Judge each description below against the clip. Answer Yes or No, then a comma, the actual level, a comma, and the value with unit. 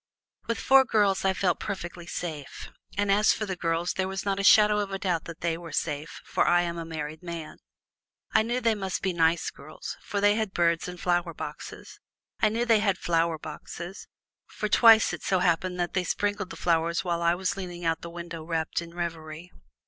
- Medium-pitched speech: Yes, medium, 175 Hz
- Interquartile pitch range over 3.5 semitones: No, average, 3.0 semitones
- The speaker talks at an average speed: No, fast, 215 wpm